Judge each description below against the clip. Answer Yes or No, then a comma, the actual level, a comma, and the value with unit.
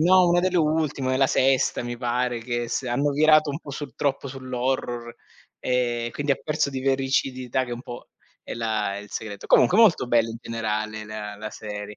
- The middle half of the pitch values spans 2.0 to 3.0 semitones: No, average, 3.4 semitones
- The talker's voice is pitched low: Yes, low, 125 Hz